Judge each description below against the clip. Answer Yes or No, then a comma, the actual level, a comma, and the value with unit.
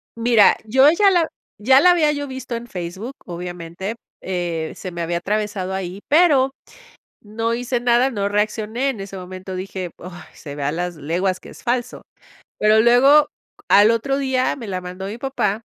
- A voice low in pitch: No, high, 210 Hz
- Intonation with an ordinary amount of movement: No, wide, 5.8 semitones